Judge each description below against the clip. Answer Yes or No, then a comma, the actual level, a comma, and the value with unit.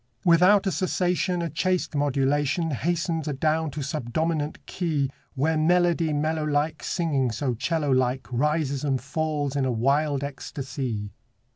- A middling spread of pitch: Yes, average, 3.2 semitones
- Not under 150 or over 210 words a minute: No, slow, 135 wpm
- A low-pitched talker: No, medium, 150 Hz